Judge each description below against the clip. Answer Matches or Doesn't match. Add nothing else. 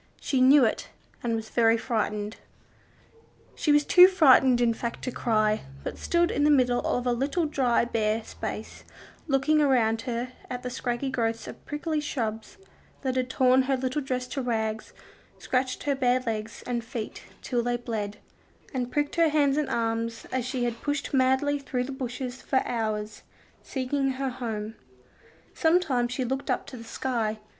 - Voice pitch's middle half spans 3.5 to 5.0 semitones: Doesn't match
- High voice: Matches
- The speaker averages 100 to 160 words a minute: Doesn't match